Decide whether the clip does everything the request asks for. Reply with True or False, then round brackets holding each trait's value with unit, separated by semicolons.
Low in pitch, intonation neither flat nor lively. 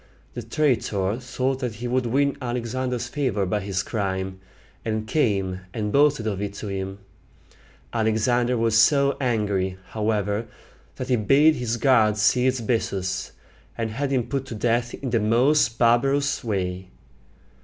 True (115 Hz; 3.6 semitones)